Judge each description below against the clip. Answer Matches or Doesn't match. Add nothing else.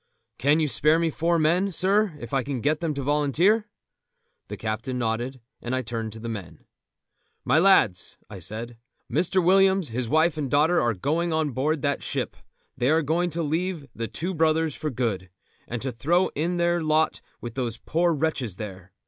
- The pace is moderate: Matches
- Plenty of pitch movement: Matches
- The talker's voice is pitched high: Doesn't match